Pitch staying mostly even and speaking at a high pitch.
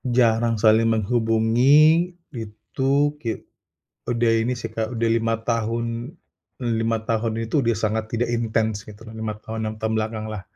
No: narrow, 1.0 semitones; low, 115 Hz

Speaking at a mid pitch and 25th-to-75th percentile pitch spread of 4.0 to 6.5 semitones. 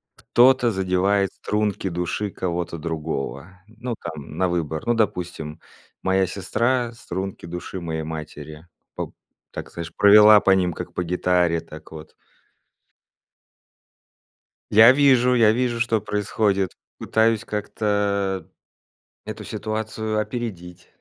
No: very low, 95 Hz; average, 4.3 semitones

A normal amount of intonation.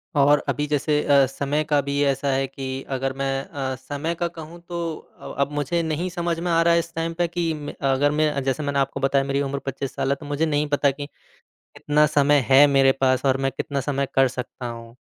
No: narrow, 2.3 semitones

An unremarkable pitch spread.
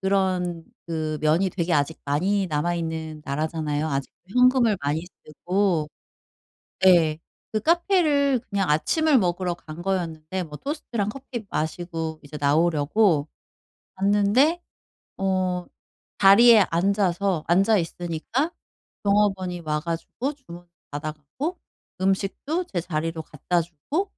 Yes: average, 4.5 semitones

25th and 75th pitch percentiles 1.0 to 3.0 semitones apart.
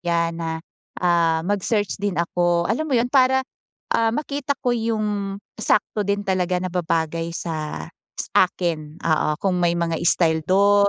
No: average, 3.9 semitones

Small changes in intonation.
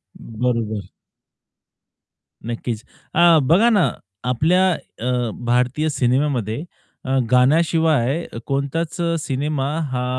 No: average, 4.7 semitones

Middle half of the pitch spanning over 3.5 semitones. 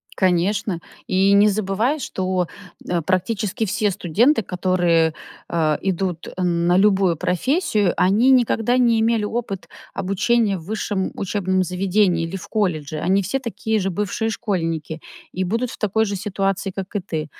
No: average, 3.2 semitones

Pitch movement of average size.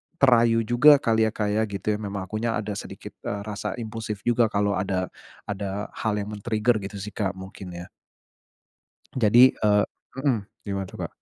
No: narrow, 2.3 semitones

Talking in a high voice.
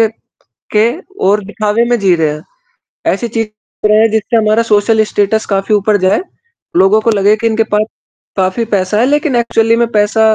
Yes: high, 215 Hz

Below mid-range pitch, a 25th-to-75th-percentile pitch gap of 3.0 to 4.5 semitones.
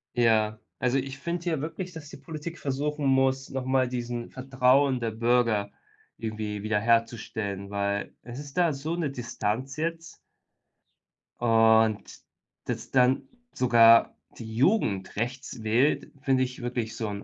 Yes: low, 125 Hz; average, 3.5 semitones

